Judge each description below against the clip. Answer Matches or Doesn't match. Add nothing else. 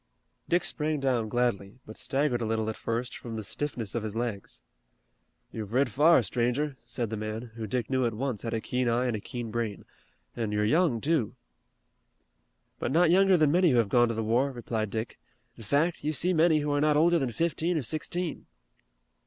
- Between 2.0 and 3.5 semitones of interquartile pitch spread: Doesn't match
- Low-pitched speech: Matches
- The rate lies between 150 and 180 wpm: Doesn't match